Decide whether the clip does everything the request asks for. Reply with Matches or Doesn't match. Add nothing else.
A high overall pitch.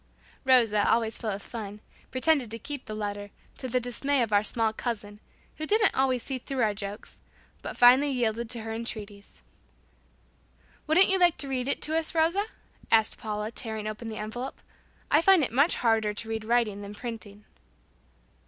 Matches